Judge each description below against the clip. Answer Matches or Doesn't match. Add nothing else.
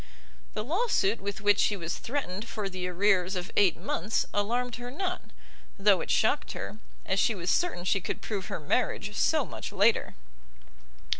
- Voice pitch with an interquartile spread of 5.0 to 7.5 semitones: Doesn't match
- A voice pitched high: Matches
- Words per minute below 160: Doesn't match